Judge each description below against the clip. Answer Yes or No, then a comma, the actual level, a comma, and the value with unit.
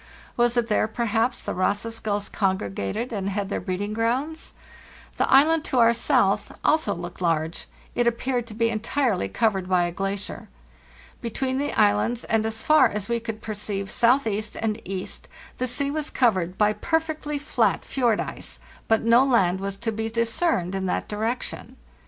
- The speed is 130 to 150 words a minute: No, average, 170 wpm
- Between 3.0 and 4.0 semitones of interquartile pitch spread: Yes, average, 3.7 semitones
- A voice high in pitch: Yes, high, 225 Hz